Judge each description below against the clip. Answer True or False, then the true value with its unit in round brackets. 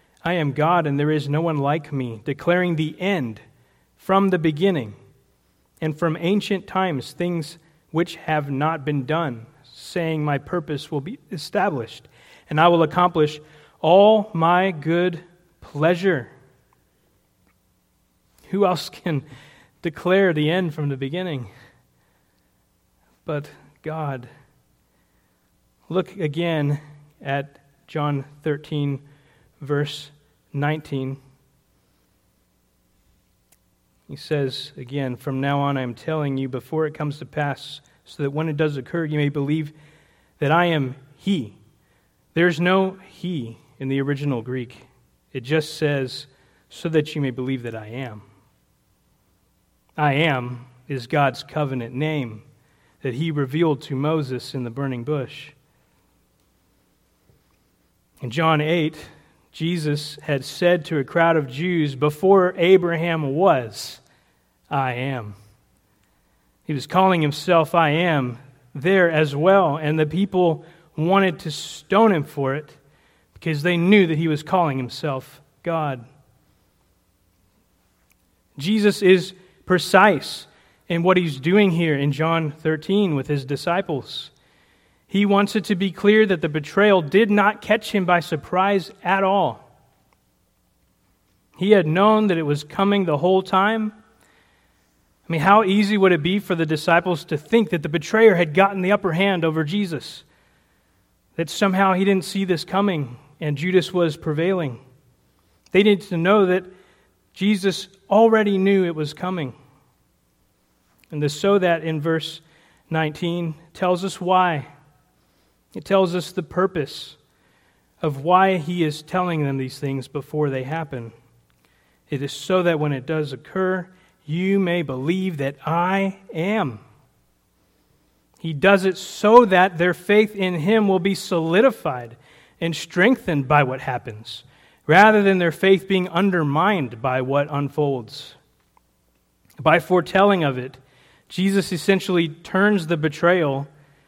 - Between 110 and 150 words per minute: True (135 wpm)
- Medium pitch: True (155 Hz)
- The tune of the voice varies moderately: True (4.6 semitones)